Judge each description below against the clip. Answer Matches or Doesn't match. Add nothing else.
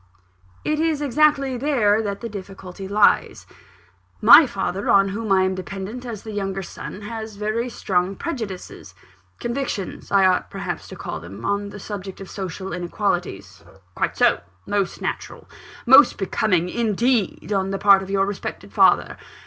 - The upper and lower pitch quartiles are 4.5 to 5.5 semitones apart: Doesn't match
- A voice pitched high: Matches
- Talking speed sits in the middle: Matches